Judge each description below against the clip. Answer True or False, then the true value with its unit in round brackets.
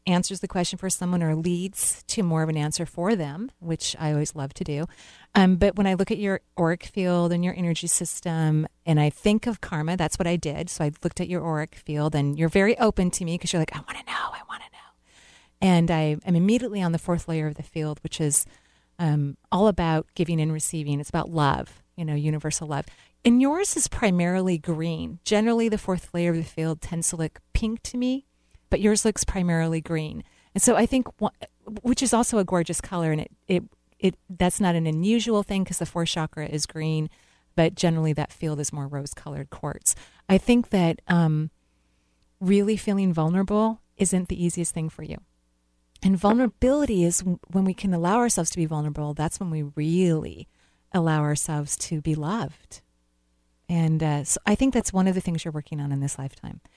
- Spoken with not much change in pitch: False (3.7 semitones)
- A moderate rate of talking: False (210 wpm)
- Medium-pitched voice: True (170 Hz)